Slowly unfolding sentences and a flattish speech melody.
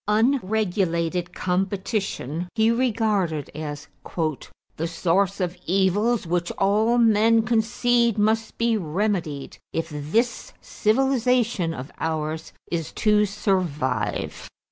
No: slow, 100 wpm; average, 5.1 semitones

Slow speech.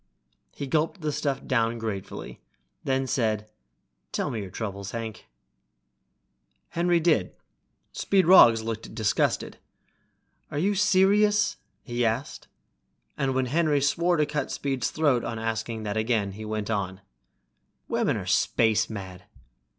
Yes: slow, 125 wpm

